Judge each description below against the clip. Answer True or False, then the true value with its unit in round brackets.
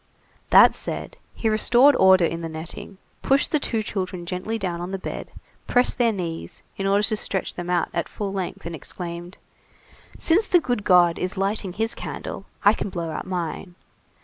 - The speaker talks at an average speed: True (185 wpm)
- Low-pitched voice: False (190 Hz)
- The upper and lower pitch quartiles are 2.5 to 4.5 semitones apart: True (3.8 semitones)